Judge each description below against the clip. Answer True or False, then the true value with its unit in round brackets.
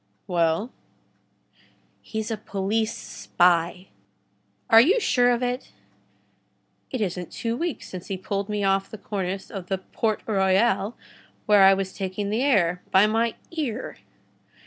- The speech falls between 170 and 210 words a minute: False (140 wpm)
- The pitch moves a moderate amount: True (3.3 semitones)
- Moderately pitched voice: False (205 Hz)